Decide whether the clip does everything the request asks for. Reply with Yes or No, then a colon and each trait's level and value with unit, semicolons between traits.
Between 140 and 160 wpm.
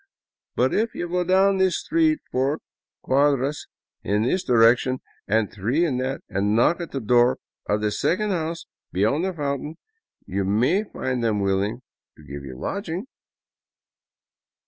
Yes: average, 150 wpm